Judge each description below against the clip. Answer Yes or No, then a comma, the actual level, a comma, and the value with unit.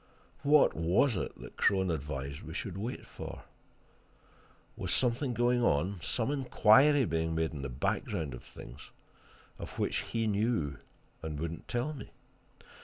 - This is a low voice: Yes, very low, 95 Hz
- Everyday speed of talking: Yes, average, 150 wpm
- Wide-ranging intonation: Yes, wide, 7.8 semitones